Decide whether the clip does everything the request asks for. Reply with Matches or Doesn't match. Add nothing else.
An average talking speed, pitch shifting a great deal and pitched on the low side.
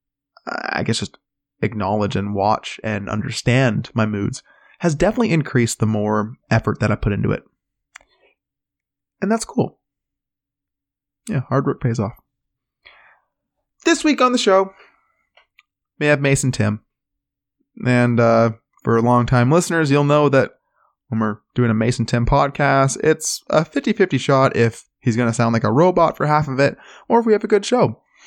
Matches